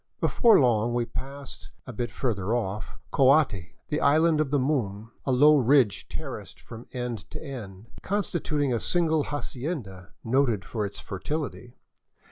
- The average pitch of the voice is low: Yes, low, 125 Hz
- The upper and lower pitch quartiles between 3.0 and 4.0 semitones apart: No, average, 5.1 semitones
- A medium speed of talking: Yes, average, 145 wpm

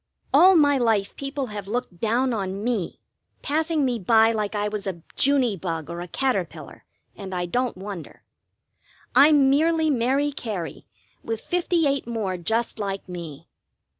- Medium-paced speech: Yes, average, 155 wpm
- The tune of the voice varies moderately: No, wide, 6.1 semitones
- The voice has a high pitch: Yes, high, 225 Hz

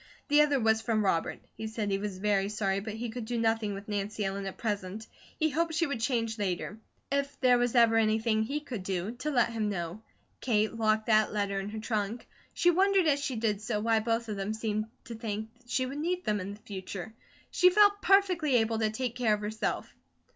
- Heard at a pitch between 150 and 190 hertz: No, high, 220 Hz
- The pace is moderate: No, fast, 220 wpm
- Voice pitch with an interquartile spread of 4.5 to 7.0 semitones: No, average, 3.2 semitones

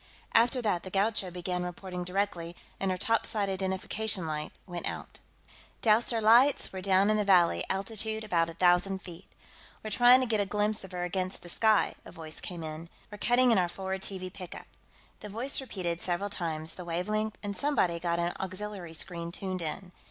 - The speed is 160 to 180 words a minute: No, average, 195 wpm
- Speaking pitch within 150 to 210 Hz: Yes, high, 190 Hz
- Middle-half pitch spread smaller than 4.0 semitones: Yes, average, 3.3 semitones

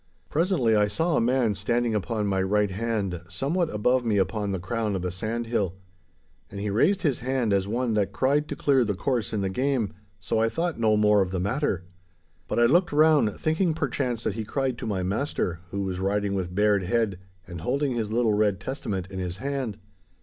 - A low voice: Yes, low, 110 Hz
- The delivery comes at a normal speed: No, fast, 210 wpm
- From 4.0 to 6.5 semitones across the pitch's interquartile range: Yes, average, 4.7 semitones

